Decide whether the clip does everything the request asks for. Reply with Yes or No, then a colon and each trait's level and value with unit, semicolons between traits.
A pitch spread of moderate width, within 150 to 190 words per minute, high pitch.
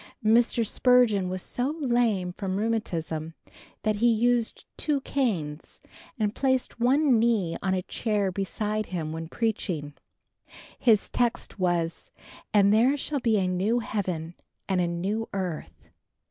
No: average, 4.7 semitones; slow, 135 wpm; high, 210 Hz